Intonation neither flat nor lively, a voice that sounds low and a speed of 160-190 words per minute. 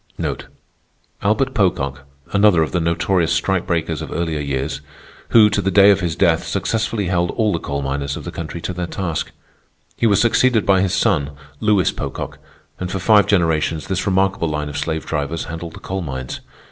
Yes: average, 4.0 semitones; very low, 85 Hz; average, 185 wpm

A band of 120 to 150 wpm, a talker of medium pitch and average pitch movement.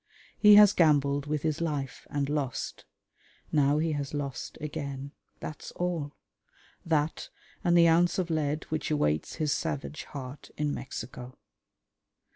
No: slow, 135 wpm; medium, 150 Hz; narrow, 2.3 semitones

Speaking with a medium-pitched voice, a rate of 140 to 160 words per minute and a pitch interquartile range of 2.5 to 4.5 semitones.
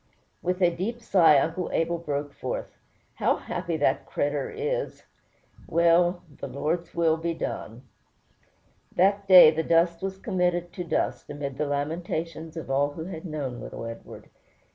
Yes: medium, 165 Hz; average, 150 wpm; average, 3.3 semitones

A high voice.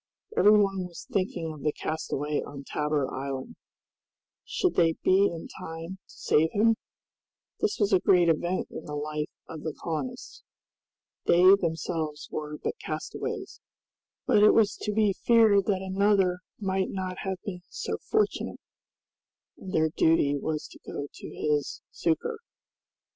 No: medium, 175 Hz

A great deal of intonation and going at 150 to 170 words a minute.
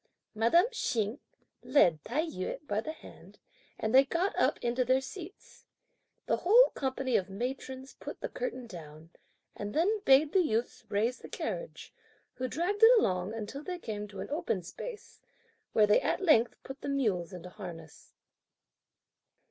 Yes: wide, 8.0 semitones; average, 160 wpm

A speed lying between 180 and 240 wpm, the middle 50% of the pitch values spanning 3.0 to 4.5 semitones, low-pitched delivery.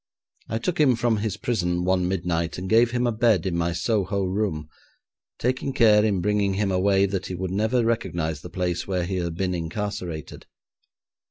Yes: average, 185 wpm; average, 3.8 semitones; very low, 95 Hz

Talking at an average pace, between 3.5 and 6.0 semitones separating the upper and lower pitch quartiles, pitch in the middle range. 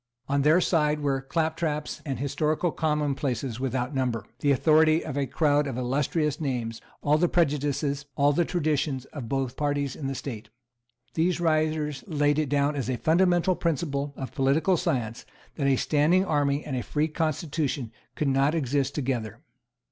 No: average, 165 wpm; narrow, 2.5 semitones; medium, 145 Hz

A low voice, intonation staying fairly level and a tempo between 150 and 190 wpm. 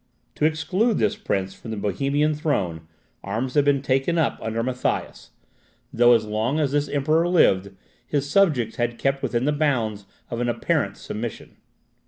No: low, 130 Hz; average, 5.0 semitones; average, 170 wpm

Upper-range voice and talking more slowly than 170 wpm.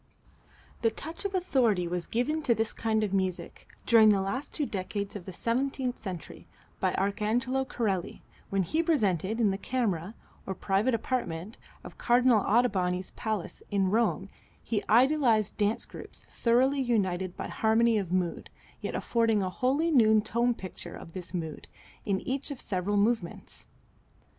Yes: high, 220 Hz; average, 155 wpm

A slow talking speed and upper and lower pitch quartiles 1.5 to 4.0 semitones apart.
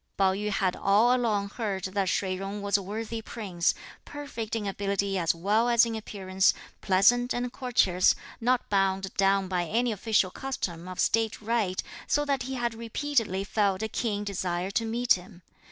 No: average, 175 wpm; average, 3.3 semitones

